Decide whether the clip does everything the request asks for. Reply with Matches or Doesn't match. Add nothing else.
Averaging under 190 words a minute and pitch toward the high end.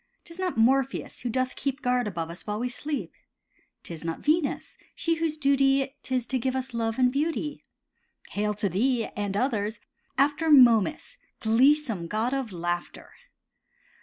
Matches